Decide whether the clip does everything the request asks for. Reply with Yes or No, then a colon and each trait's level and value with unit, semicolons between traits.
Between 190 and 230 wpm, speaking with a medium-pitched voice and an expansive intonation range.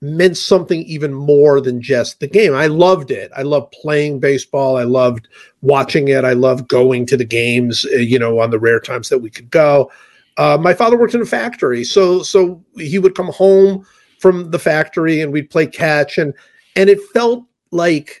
Yes: average, 200 wpm; medium, 155 Hz; wide, 5.8 semitones